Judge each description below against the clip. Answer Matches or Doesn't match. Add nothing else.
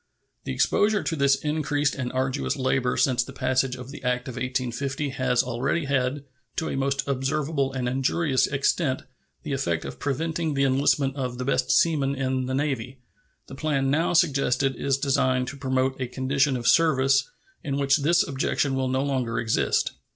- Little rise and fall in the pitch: Matches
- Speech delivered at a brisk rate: Doesn't match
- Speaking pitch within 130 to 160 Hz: Matches